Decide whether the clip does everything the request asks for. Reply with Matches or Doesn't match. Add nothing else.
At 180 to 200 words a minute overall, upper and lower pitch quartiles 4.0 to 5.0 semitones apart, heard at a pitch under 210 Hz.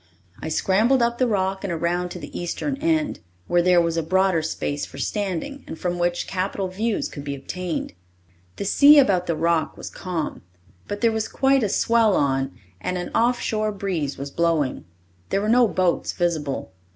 Matches